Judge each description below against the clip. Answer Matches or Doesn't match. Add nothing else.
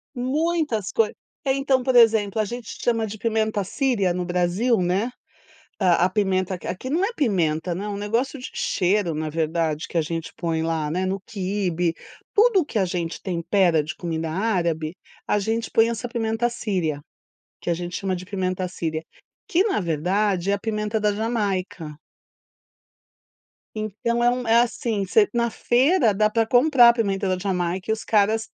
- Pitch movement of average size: Matches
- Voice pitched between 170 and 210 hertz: Matches